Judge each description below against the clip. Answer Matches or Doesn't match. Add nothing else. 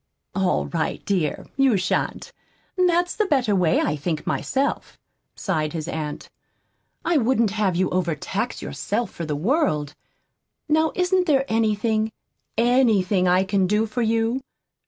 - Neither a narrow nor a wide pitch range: Doesn't match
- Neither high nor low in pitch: Doesn't match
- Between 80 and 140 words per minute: Matches